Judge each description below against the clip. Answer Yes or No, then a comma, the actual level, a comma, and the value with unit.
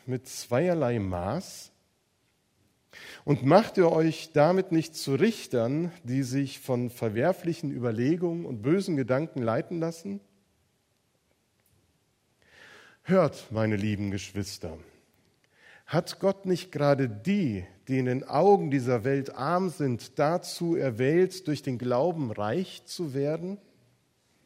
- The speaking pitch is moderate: Yes, medium, 145 Hz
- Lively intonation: Yes, wide, 6.1 semitones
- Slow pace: Yes, slow, 115 wpm